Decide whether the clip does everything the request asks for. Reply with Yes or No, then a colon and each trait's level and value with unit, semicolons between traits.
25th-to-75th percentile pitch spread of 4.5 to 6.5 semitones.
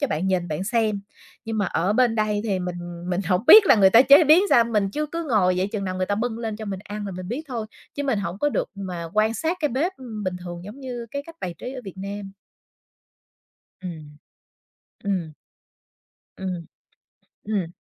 Yes: average, 4.8 semitones